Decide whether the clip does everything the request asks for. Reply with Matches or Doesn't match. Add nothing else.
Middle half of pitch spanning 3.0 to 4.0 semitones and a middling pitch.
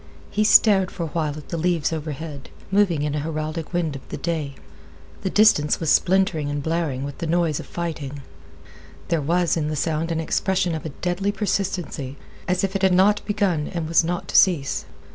Matches